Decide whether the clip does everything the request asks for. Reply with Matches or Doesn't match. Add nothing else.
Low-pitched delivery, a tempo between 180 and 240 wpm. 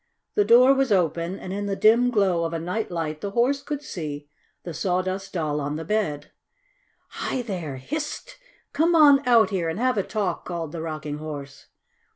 Doesn't match